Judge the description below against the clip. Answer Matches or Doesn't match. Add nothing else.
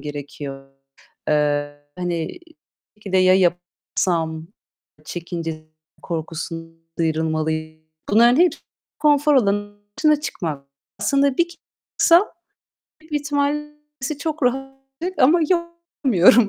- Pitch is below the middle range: Doesn't match